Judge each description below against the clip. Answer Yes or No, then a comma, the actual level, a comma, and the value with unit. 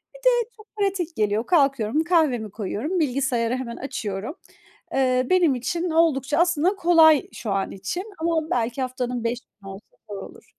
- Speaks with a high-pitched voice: Yes, very high, 270 Hz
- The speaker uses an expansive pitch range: Yes, wide, 6.3 semitones